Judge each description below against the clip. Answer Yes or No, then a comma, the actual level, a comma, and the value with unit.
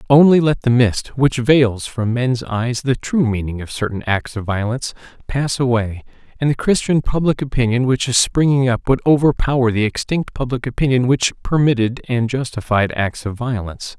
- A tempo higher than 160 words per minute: Yes, average, 175 wpm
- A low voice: Yes, low, 125 Hz